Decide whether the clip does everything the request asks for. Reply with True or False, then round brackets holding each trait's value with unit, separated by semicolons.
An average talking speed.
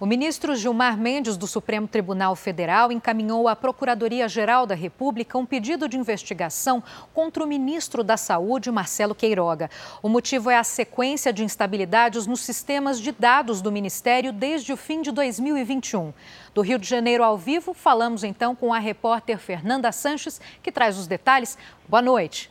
True (165 wpm)